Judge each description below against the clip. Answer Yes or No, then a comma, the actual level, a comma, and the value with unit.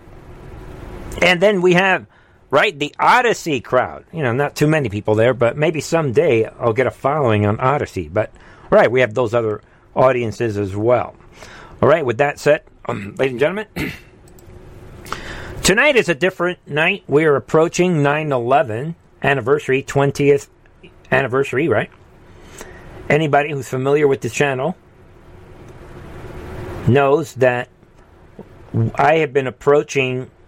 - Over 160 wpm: No, slow, 135 wpm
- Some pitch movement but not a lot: Yes, average, 3.9 semitones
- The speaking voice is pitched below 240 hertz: Yes, low, 135 Hz